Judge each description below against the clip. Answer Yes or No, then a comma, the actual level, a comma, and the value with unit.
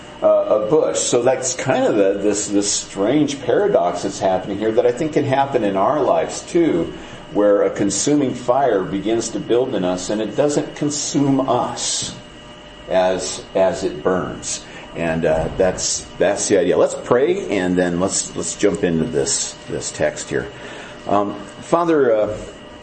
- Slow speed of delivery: No, average, 165 wpm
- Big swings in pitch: Yes, wide, 6.9 semitones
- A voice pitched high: No, low, 100 Hz